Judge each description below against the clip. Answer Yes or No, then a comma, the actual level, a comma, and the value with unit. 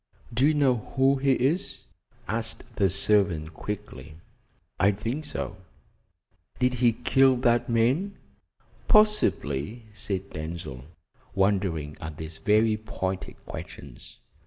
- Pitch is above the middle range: No, low, 105 Hz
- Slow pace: Yes, slow, 110 wpm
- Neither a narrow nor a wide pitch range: No, wide, 5.7 semitones